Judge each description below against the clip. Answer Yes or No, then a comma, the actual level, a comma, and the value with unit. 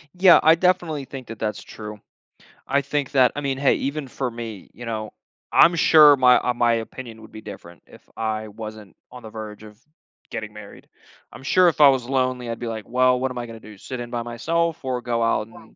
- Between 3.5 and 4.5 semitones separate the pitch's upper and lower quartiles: Yes, average, 3.8 semitones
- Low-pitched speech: Yes, low, 120 Hz